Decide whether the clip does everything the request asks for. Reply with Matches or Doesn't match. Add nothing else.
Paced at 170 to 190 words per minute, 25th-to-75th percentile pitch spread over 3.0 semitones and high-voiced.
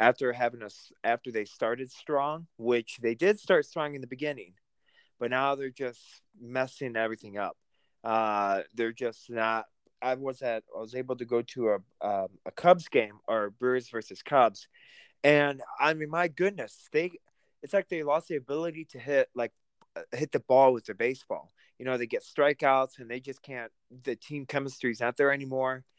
Doesn't match